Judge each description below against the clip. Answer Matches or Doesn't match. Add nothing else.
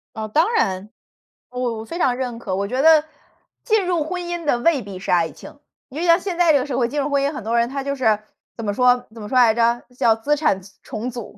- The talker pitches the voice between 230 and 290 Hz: Matches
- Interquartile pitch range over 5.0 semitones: Matches